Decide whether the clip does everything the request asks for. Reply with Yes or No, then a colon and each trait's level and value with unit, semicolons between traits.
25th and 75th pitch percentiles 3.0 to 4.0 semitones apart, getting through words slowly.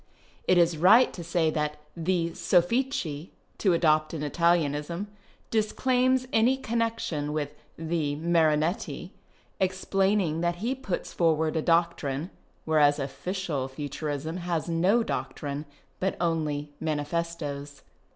Yes: average, 3.7 semitones; slow, 130 wpm